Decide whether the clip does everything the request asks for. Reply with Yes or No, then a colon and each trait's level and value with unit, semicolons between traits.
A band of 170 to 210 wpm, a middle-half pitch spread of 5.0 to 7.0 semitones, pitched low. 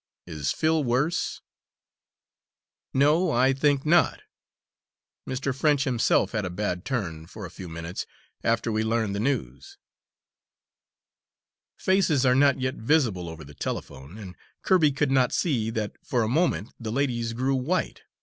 No: average, 145 wpm; wide, 5.6 semitones; low, 125 Hz